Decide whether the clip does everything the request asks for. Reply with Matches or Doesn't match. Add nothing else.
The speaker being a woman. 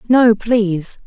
Matches